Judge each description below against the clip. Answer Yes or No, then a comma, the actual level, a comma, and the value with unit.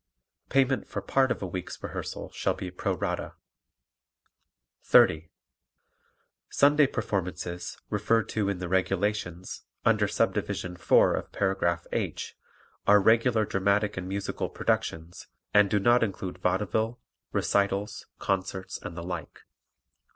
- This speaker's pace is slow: Yes, slow, 120 wpm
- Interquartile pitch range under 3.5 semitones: Yes, average, 2.8 semitones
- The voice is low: Yes, low, 100 Hz